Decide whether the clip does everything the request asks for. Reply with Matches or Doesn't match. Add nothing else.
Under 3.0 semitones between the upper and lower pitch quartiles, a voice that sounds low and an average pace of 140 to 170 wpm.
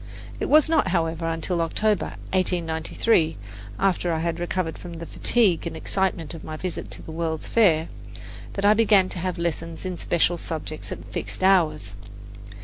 Doesn't match